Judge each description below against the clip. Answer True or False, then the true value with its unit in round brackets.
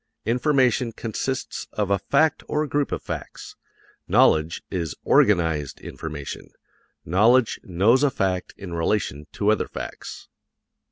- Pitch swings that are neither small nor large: False (7.2 semitones)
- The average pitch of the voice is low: True (105 Hz)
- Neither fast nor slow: False (125 wpm)